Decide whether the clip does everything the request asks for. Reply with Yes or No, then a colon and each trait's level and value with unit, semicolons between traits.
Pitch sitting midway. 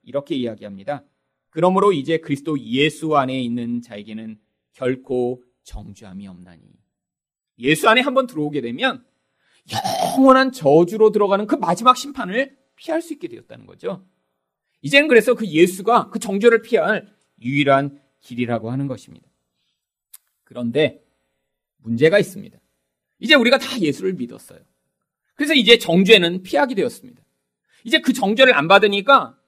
Yes: medium, 170 Hz